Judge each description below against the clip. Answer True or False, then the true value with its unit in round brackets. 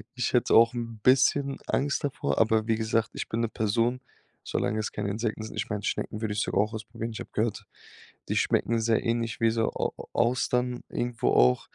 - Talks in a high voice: False (115 Hz)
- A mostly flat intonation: True (1.7 semitones)